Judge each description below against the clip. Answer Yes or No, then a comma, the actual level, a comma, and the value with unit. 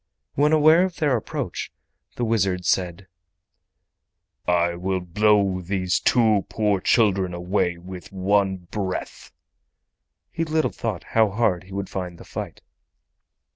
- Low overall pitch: Yes, very low, 95 Hz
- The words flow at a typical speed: No, slow, 130 wpm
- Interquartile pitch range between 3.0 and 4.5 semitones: Yes, average, 3.5 semitones